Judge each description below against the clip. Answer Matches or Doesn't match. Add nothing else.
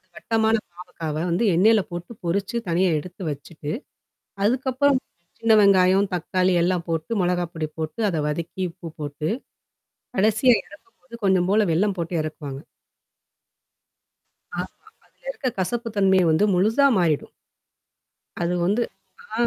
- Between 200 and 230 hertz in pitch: Doesn't match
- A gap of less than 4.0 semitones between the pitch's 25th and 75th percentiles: Doesn't match